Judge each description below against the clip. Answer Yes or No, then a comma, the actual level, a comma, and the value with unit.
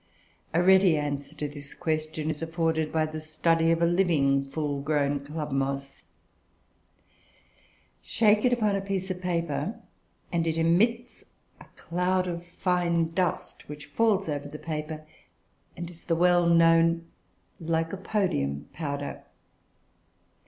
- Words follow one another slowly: Yes, slow, 130 wpm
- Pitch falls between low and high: Yes, medium, 165 Hz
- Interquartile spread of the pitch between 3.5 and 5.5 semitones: No, average, 3.0 semitones